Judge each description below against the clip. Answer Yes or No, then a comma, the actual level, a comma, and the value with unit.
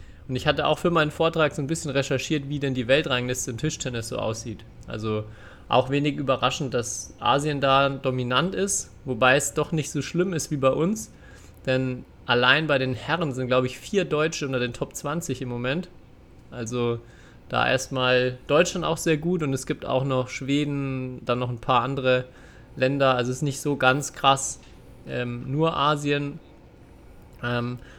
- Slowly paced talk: No, average, 180 wpm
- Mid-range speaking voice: No, low, 130 Hz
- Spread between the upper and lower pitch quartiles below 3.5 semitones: Yes, average, 3.0 semitones